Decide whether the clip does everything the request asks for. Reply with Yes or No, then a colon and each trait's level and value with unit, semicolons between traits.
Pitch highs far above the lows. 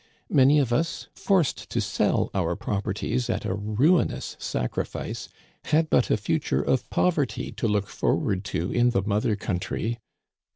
Yes: wide, 5.8 semitones